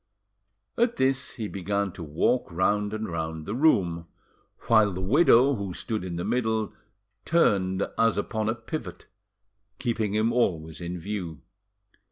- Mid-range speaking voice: No, low, 105 Hz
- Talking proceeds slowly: No, average, 145 wpm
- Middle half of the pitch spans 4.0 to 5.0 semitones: Yes, average, 4.3 semitones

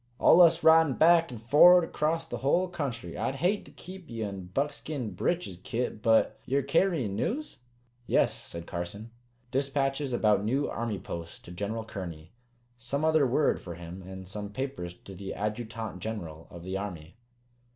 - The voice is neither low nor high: No, low, 115 Hz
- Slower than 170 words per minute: Yes, average, 160 wpm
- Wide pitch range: Yes, wide, 7.4 semitones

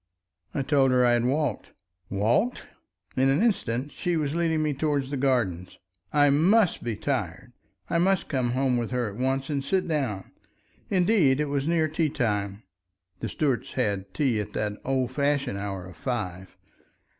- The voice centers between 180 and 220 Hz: No, low, 135 Hz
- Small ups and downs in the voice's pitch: No, average, 4.7 semitones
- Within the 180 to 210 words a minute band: No, average, 170 wpm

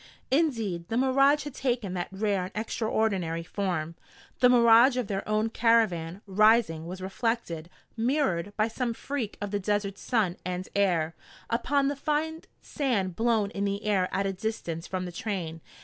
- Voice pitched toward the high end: Yes, high, 210 Hz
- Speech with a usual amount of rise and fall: Yes, average, 4.4 semitones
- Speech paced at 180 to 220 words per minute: No, average, 165 wpm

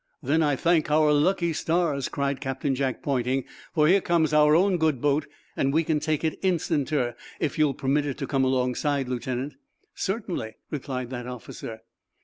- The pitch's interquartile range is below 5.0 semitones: Yes, average, 3.2 semitones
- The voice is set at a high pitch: No, medium, 145 Hz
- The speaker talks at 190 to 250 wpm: No, average, 170 wpm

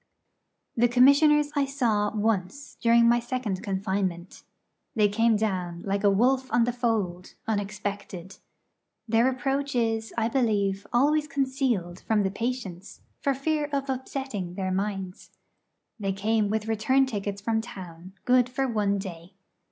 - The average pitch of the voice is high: Yes, high, 220 Hz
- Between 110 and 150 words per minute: Yes, average, 140 wpm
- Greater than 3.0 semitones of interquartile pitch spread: Yes, average, 4.5 semitones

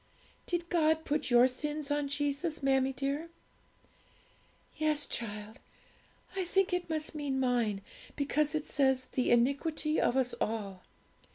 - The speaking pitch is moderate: No, very high, 285 Hz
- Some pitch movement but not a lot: Yes, average, 3.4 semitones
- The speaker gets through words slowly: Yes, slow, 130 wpm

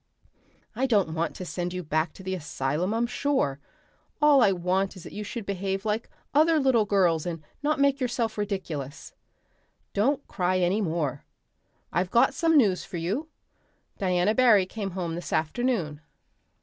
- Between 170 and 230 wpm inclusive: No, average, 160 wpm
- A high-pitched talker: Yes, high, 195 Hz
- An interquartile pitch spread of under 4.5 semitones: No, wide, 5.4 semitones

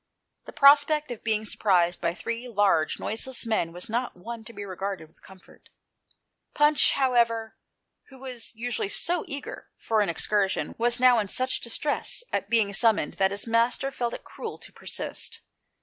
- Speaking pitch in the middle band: No, high, 230 Hz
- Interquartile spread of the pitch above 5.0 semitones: No, average, 4.0 semitones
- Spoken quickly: No, average, 165 wpm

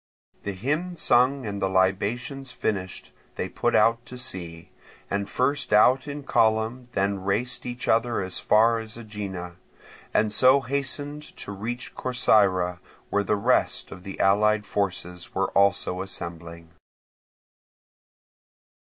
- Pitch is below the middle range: Yes, low, 105 Hz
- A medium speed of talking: No, slow, 130 wpm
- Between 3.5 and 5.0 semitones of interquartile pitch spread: Yes, average, 4.6 semitones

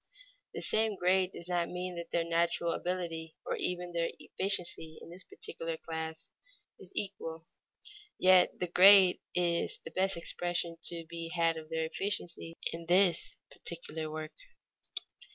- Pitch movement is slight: Yes, narrow, 1.6 semitones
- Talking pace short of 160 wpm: Yes, average, 145 wpm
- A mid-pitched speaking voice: Yes, medium, 170 Hz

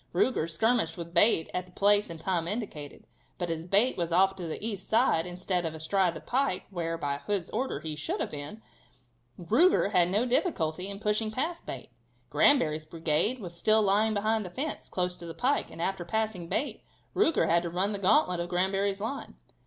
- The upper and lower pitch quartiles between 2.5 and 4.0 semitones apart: No, average, 4.4 semitones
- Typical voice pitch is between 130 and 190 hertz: Yes, medium, 185 Hz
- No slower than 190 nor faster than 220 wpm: Yes, average, 200 wpm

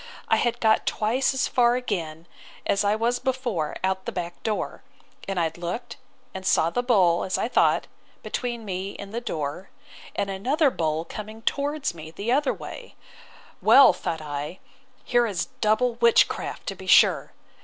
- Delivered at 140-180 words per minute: Yes, average, 170 wpm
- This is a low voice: No, high, 210 Hz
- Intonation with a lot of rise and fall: Yes, wide, 5.8 semitones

